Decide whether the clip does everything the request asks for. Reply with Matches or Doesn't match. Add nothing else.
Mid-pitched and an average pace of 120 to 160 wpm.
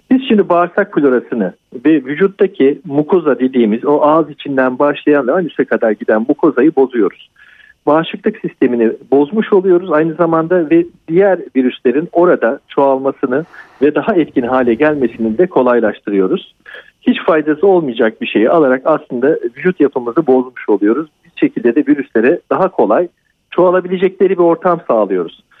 Matches